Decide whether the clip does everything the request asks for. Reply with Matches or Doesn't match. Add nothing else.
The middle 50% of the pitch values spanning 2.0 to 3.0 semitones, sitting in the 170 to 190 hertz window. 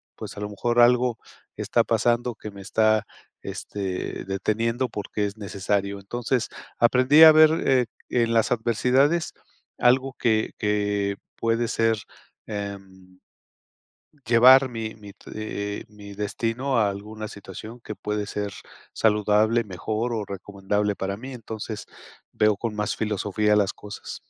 Doesn't match